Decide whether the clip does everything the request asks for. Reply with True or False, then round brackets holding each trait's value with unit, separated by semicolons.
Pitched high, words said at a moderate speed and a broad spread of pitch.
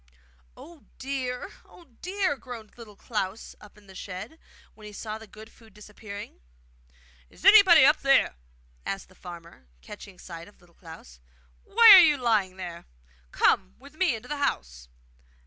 True (215 Hz; 160 wpm; 6.7 semitones)